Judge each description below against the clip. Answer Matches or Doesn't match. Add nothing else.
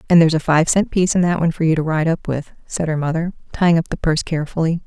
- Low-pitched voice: Doesn't match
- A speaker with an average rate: Doesn't match